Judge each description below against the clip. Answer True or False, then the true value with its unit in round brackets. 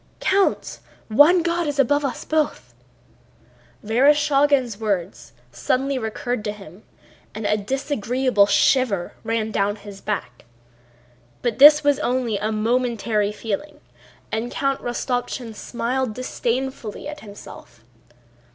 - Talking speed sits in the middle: False (110 wpm)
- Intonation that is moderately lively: True (4.6 semitones)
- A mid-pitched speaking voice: False (240 Hz)